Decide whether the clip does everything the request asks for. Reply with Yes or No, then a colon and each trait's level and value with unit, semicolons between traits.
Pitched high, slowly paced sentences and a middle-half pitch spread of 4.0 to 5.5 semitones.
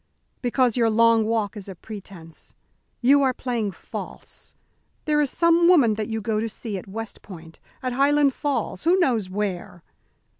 No: high, 225 Hz; average, 165 wpm; average, 4.8 semitones